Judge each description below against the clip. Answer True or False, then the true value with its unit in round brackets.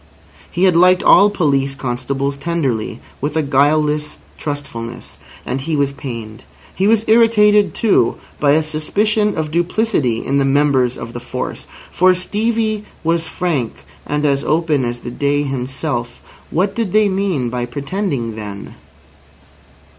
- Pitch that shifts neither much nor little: False (5.8 semitones)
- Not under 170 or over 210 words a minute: False (145 wpm)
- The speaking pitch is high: False (150 Hz)